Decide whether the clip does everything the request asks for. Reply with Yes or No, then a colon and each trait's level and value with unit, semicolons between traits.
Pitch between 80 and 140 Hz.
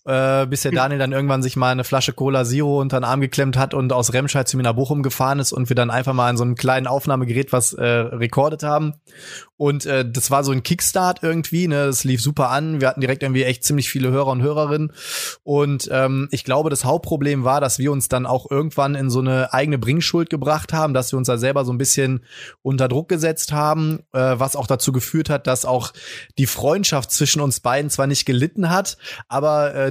Yes: low, 135 Hz